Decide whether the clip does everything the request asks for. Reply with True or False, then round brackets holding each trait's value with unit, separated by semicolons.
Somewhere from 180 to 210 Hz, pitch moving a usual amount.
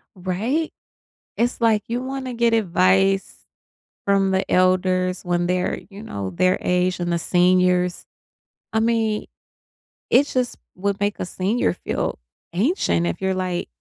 True (190 Hz; 3.6 semitones)